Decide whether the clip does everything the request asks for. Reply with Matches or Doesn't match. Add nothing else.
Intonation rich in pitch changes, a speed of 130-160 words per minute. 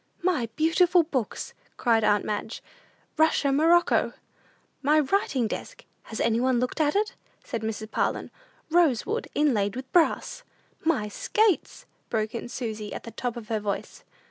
Matches